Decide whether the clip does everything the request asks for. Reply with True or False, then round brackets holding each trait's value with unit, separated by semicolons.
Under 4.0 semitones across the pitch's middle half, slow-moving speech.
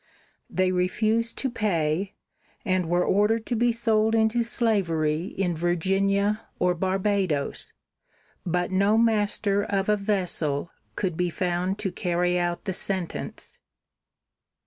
True (3.2 semitones; 125 wpm)